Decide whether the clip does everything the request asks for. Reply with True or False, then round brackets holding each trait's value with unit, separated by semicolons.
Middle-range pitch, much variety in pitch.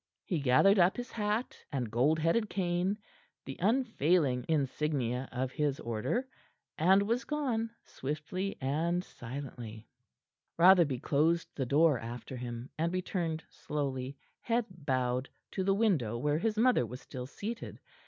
True (155 Hz; 7.0 semitones)